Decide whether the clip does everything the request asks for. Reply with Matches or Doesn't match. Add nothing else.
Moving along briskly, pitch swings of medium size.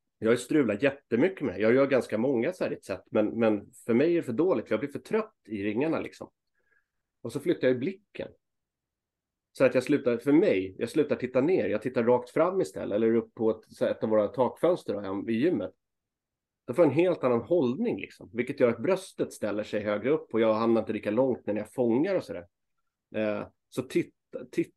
Matches